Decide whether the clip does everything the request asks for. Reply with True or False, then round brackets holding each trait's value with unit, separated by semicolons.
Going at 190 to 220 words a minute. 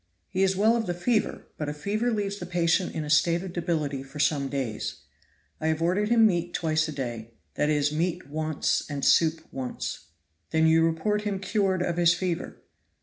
True (200 wpm)